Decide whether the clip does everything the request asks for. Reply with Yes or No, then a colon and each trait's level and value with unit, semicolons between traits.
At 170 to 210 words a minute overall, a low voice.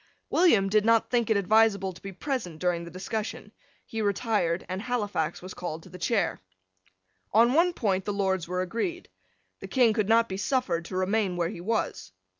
No: average, 190 wpm; high, 200 Hz